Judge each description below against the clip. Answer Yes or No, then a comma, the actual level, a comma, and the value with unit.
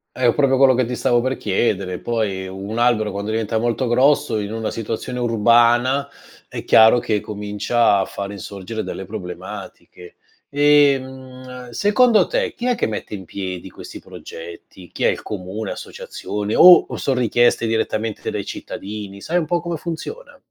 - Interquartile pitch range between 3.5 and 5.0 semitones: Yes, average, 4.2 semitones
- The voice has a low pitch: Yes, low, 115 Hz